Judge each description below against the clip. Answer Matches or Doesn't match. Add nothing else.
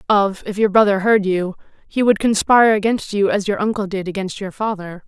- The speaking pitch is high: Matches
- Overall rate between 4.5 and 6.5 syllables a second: Matches